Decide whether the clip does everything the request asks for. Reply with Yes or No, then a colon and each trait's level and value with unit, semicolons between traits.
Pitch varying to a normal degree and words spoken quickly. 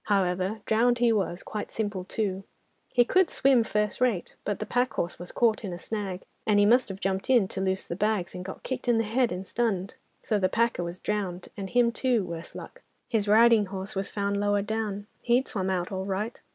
Yes: average, 3.3 semitones; fast, 220 wpm